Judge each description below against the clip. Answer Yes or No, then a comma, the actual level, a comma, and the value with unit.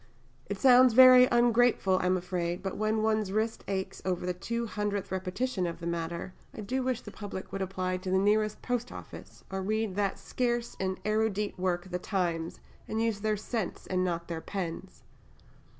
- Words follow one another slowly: No, average, 180 wpm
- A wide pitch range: No, average, 3.3 semitones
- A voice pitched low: No, high, 195 Hz